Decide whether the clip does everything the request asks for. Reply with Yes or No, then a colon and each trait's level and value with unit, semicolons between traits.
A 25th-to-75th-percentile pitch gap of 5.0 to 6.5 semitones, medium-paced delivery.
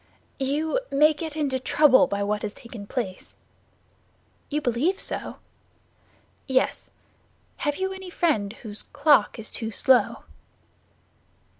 No: wide, 5.5 semitones; slow, 120 wpm